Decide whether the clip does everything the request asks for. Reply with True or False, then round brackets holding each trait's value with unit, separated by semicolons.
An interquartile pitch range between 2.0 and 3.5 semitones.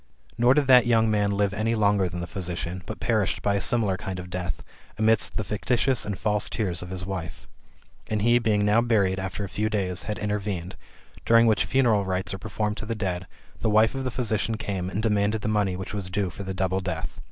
True (2.8 semitones)